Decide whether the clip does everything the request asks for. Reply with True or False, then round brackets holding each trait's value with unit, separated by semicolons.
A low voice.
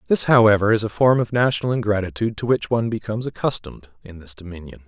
True (105 Hz)